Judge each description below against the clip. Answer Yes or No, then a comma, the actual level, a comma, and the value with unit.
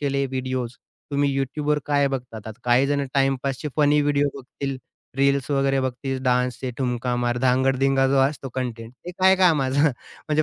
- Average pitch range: No, narrow, 1.9 semitones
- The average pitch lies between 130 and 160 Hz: Yes, low, 135 Hz